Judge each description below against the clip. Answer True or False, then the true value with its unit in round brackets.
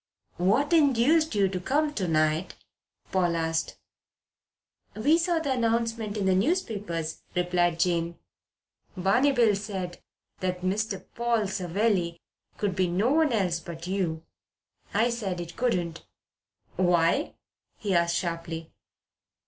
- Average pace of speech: False (125 wpm)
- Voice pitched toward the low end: False (190 Hz)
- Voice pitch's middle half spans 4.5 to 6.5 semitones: True (5.2 semitones)